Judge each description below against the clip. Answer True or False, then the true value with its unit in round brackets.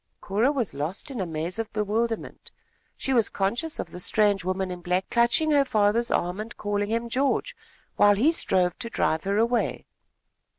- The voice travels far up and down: False (3.8 semitones)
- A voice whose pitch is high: True (210 Hz)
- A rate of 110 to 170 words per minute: False (180 wpm)